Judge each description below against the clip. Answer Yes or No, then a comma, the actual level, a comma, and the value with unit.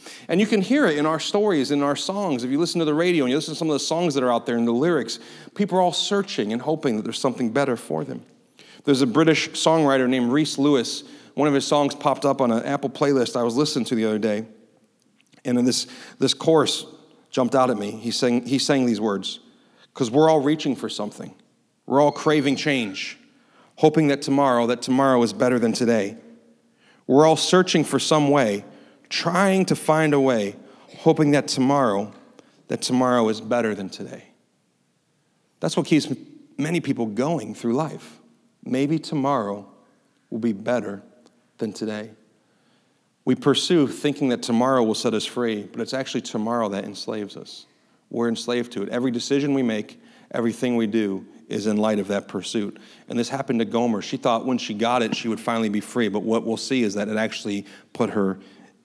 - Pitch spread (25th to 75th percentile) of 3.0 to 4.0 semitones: No, average, 5.0 semitones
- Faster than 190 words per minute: Yes, average, 200 wpm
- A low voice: Yes, low, 130 Hz